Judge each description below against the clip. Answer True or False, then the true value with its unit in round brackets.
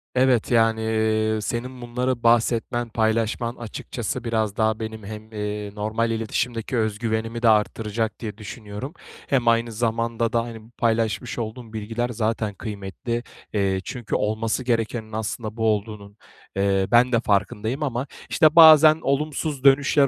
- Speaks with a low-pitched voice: True (115 Hz)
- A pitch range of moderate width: False (1.7 semitones)